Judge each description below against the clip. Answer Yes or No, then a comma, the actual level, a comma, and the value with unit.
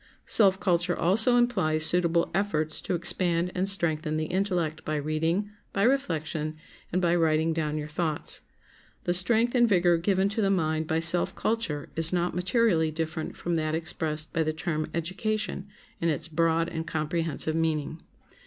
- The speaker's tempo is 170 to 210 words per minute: No, average, 160 wpm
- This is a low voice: No, medium, 170 Hz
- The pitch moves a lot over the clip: No, average, 3.0 semitones